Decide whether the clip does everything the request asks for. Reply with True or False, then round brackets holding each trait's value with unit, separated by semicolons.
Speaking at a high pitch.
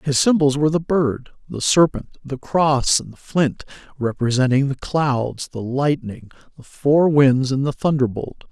False (140 Hz)